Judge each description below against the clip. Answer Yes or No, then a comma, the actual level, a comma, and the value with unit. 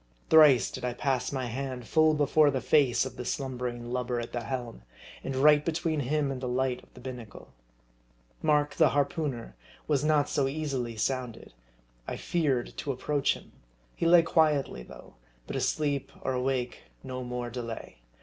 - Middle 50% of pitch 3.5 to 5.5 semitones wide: No, average, 3.0 semitones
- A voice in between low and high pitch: No, low, 130 Hz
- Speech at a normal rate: Yes, average, 180 wpm